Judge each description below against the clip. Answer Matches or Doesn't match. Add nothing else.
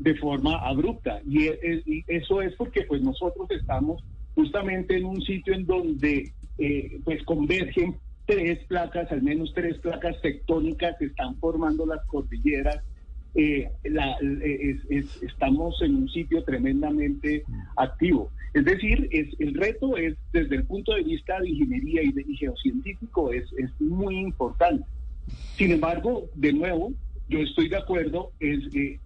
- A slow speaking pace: Doesn't match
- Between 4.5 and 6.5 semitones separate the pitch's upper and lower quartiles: Matches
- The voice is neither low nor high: Matches